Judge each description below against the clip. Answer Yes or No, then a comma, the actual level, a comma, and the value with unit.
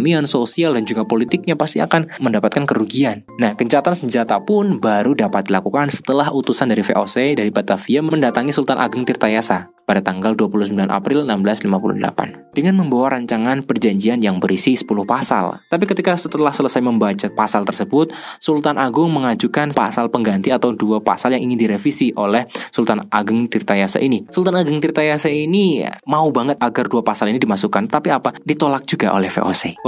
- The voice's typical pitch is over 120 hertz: Yes, low, 135 Hz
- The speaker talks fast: Yes, fast, 155 wpm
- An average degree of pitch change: No, wide, 5.8 semitones